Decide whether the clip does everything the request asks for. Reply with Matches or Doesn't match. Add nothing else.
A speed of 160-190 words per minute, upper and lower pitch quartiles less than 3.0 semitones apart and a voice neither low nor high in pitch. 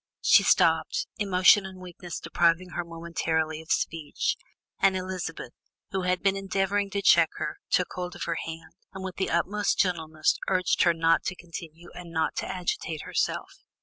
Matches